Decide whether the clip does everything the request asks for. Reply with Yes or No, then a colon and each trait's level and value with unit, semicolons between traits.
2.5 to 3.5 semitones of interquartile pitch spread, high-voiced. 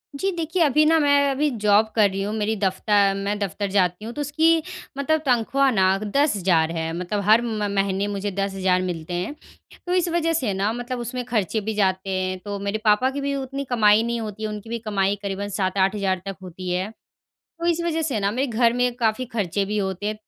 No: average, 4.7 semitones; high, 210 Hz